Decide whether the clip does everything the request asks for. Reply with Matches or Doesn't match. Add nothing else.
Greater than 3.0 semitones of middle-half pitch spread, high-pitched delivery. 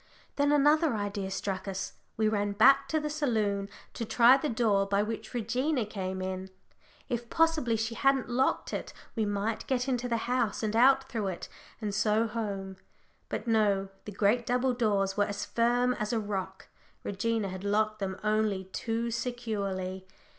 Matches